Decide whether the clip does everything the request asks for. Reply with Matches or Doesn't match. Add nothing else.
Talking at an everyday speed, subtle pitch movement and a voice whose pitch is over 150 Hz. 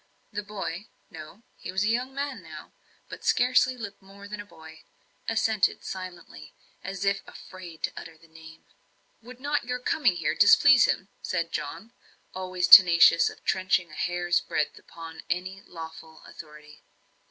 Doesn't match